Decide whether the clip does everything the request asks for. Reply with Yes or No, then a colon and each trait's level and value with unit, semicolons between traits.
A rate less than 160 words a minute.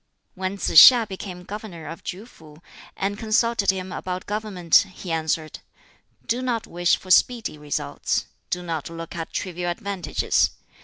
Yes: average, 150 wpm